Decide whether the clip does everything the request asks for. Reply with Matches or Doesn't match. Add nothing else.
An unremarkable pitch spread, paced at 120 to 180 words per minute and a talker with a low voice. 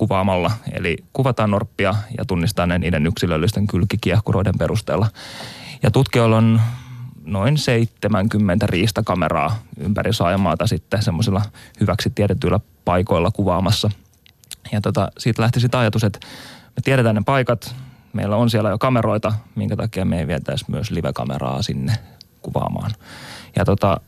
Matches